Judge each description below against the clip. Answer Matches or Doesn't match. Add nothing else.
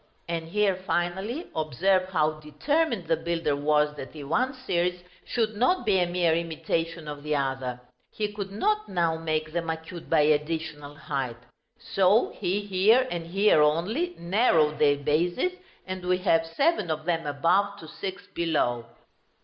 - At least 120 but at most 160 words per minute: Matches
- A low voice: Doesn't match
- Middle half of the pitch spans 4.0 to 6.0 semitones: Matches